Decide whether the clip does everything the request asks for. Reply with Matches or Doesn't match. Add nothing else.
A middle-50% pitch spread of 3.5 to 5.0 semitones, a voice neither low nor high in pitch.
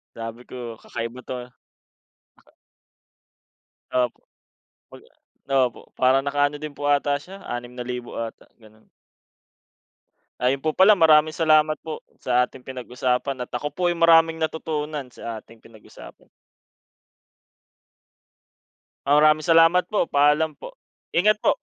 Matches